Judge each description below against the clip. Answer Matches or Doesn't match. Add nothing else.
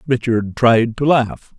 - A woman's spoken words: Doesn't match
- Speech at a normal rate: Matches